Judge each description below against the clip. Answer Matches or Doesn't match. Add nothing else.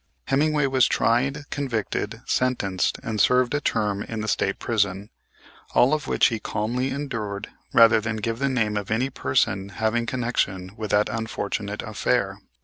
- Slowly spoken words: Doesn't match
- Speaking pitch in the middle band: Doesn't match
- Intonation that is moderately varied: Matches